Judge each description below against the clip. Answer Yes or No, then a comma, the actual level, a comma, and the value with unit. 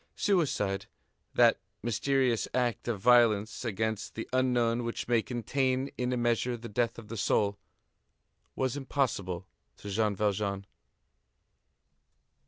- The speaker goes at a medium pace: No, slow, 120 wpm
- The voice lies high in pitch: No, low, 115 Hz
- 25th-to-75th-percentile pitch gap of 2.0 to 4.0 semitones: Yes, average, 3.1 semitones